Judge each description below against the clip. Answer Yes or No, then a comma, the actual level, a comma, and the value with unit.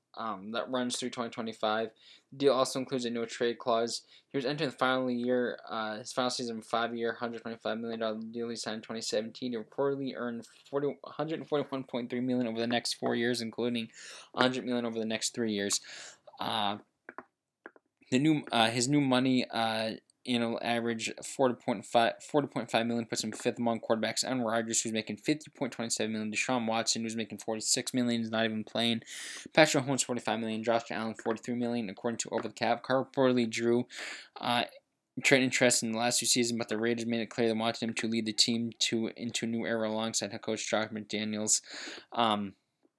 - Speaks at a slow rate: No, average, 190 wpm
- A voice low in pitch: Yes, low, 115 Hz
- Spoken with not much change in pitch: Yes, narrow, 1.7 semitones